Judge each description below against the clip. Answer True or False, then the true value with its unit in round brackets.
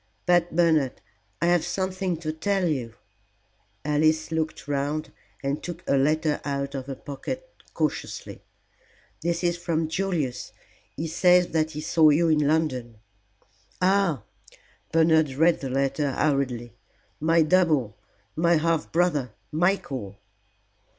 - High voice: False (155 Hz)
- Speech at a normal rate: False (125 wpm)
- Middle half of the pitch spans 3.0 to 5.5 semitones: True (3.6 semitones)